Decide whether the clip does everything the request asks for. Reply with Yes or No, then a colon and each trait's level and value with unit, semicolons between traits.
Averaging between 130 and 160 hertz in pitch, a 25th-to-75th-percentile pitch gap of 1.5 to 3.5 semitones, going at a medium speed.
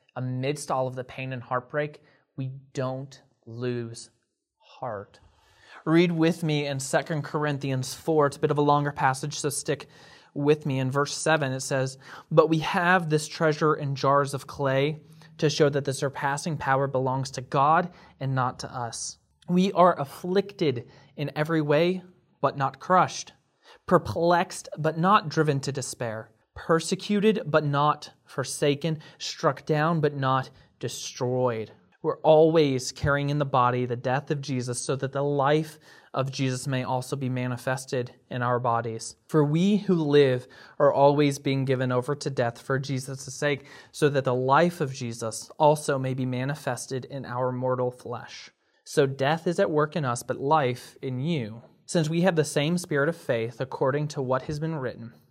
Yes: medium, 140 Hz; average, 3.2 semitones; average, 170 wpm